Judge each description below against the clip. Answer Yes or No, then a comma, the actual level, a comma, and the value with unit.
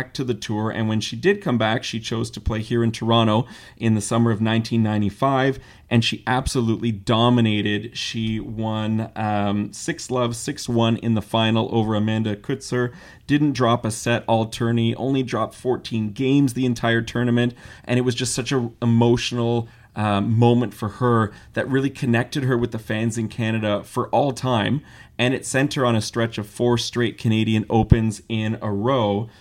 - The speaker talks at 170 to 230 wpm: Yes, average, 180 wpm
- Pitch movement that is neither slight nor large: No, narrow, 2.0 semitones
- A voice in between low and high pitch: No, low, 115 Hz